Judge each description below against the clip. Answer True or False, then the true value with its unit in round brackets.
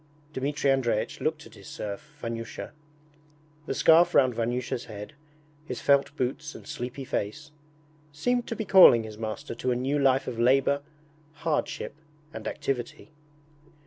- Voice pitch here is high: False (135 Hz)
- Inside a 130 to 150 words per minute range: True (145 wpm)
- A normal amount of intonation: True (3.9 semitones)